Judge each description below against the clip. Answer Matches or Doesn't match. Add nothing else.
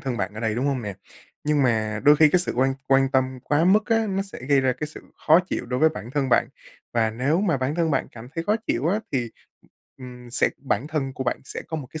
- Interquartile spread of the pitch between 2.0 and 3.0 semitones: Doesn't match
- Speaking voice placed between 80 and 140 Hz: Matches